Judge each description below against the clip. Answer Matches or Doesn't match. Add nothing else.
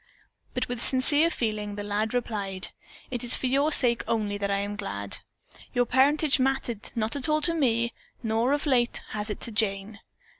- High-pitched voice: Matches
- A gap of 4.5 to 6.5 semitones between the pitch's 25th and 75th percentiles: Doesn't match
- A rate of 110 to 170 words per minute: Doesn't match